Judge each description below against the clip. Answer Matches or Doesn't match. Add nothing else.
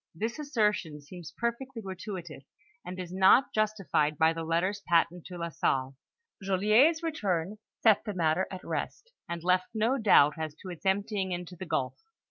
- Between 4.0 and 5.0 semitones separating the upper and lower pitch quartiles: Matches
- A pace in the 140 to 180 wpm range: Matches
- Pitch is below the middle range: Doesn't match